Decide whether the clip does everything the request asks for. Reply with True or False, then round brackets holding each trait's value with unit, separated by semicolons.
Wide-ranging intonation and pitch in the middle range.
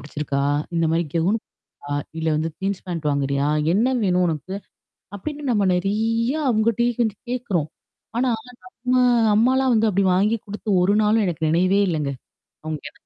False (5.8 semitones; 195 Hz)